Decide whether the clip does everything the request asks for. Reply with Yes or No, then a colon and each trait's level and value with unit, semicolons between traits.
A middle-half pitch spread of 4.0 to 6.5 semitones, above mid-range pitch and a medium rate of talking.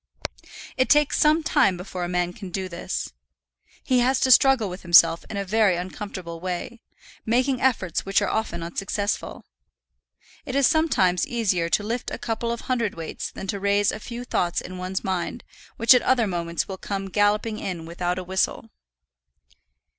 Yes: average, 4.8 semitones; high, 200 Hz; average, 170 wpm